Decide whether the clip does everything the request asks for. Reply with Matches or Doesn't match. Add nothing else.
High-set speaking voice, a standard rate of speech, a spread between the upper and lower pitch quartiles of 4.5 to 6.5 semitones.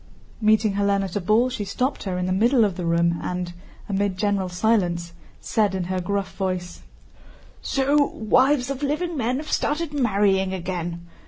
Matches